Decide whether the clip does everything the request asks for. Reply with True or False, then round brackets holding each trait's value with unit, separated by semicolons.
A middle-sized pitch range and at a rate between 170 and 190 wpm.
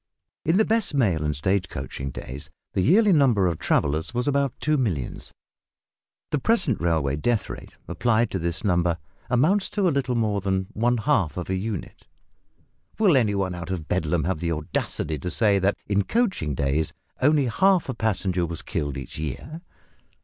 False (8.4 semitones; 180 wpm)